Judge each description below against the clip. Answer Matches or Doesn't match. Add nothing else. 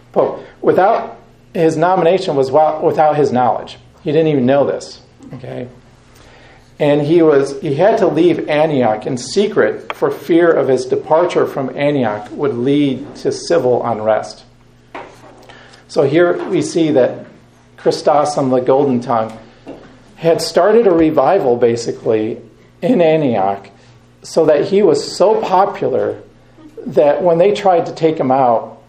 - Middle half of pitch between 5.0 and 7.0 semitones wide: Matches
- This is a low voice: Doesn't match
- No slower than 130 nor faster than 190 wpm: Matches